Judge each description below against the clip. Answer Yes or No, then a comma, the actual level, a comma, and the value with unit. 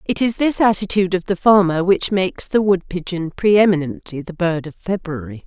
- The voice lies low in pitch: No, medium, 180 Hz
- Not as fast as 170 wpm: No, average, 185 wpm